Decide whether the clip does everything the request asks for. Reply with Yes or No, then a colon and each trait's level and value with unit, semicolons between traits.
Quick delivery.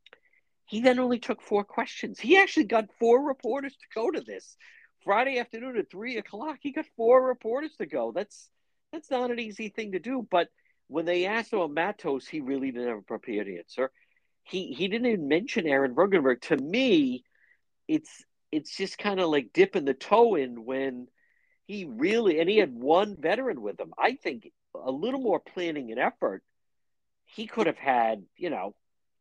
No: average, 190 wpm